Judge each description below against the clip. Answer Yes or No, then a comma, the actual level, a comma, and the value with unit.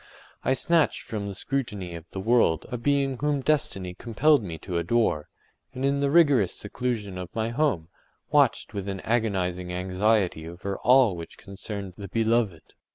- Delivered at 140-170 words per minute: Yes, average, 160 wpm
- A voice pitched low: Yes, low, 105 Hz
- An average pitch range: No, wide, 5.8 semitones